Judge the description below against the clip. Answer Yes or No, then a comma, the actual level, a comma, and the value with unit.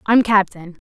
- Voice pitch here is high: Yes, high, 200 Hz